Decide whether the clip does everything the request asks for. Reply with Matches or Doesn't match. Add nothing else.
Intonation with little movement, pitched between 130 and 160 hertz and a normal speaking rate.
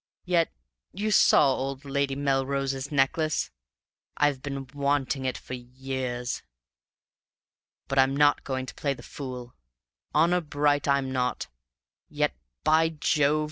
Doesn't match